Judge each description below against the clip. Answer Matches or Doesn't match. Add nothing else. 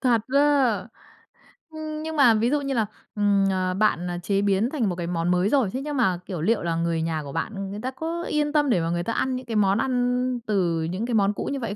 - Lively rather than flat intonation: Matches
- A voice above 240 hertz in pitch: Doesn't match